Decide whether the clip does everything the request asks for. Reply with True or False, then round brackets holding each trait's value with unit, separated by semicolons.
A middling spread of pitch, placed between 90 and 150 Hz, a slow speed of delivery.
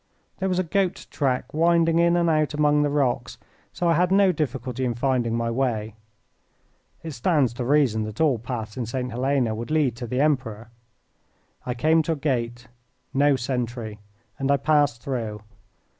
False (4.5 semitones; 135 Hz; 175 wpm)